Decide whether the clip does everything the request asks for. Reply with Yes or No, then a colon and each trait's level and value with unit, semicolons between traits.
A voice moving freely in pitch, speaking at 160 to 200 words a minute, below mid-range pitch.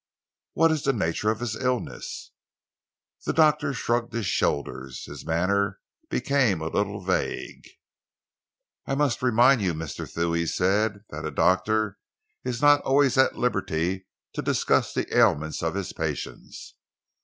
No: wide, 7.0 semitones; average, 145 wpm; low, 105 Hz